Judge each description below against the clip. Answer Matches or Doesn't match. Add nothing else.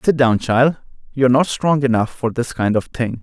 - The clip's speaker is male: Matches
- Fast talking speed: Matches